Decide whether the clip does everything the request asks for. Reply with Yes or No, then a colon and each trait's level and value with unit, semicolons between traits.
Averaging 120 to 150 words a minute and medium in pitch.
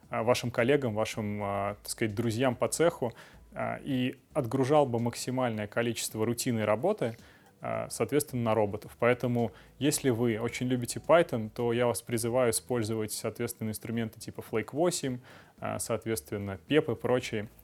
No: average, 125 wpm; low, 120 Hz